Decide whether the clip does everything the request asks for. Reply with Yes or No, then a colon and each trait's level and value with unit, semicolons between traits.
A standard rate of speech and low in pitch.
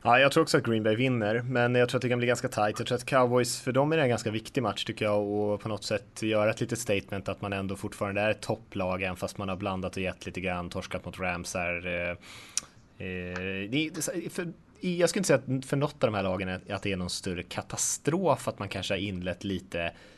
No: fast, 230 wpm; low, 105 Hz